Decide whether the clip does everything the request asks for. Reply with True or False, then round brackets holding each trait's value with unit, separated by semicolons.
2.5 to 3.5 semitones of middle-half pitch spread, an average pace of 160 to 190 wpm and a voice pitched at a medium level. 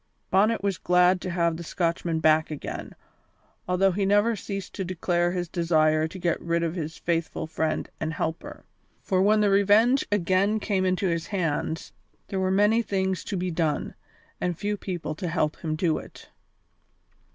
True (3.0 semitones; 175 wpm; 180 Hz)